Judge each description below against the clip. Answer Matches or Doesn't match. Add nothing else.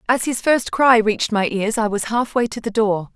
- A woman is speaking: Matches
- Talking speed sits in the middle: Doesn't match